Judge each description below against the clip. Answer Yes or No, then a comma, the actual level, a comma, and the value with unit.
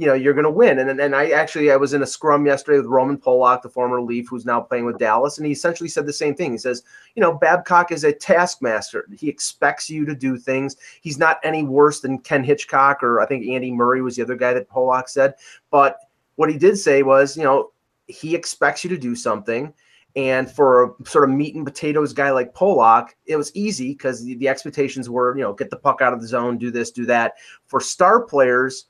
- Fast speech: Yes, fast, 240 wpm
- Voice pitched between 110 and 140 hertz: Yes, low, 135 Hz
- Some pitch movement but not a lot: Yes, average, 3.1 semitones